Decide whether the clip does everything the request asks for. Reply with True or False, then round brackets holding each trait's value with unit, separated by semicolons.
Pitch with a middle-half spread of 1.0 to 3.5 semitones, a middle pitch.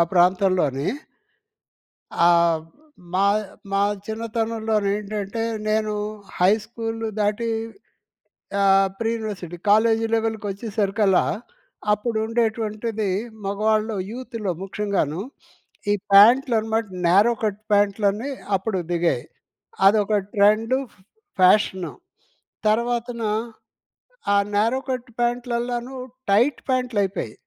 False (2.6 semitones; 215 Hz)